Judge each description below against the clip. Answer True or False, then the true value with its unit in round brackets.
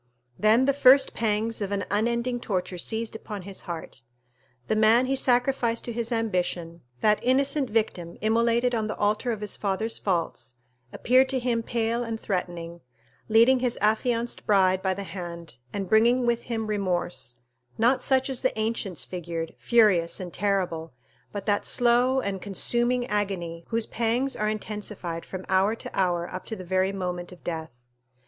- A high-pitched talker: True (215 Hz)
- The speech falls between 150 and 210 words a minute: True (165 wpm)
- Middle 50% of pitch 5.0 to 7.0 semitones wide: False (4.3 semitones)